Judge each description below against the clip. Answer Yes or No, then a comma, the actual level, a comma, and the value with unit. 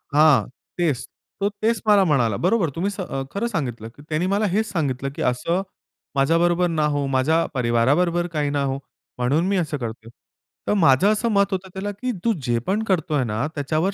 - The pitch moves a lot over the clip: Yes, wide, 6.3 semitones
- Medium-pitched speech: Yes, medium, 160 Hz